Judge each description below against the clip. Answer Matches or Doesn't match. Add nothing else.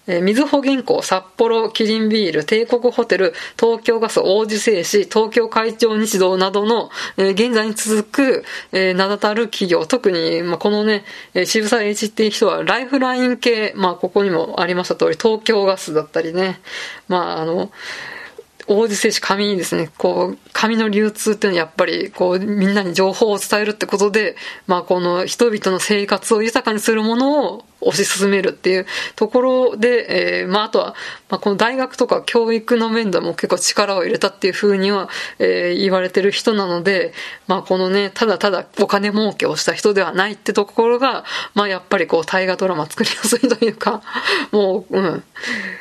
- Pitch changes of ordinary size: Matches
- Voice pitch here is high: Matches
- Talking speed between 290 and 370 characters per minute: Matches